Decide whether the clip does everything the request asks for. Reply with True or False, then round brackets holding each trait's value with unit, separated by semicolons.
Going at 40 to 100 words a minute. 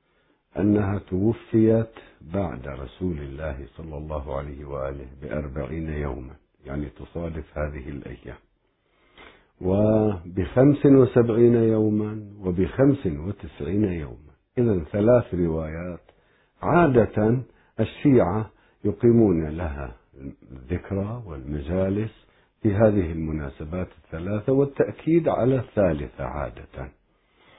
True (85 wpm)